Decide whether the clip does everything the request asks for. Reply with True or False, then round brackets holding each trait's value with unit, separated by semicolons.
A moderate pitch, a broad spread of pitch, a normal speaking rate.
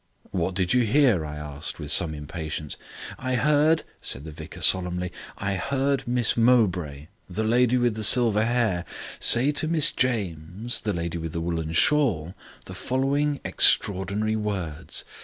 False (105 Hz; 7.0 semitones; 155 wpm)